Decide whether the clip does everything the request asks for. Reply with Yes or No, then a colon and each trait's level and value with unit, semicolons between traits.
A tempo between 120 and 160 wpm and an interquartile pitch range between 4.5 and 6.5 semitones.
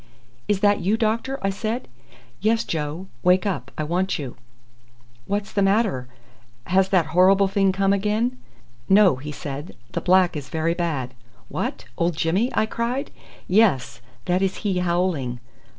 No: average, 150 wpm; average, 4.0 semitones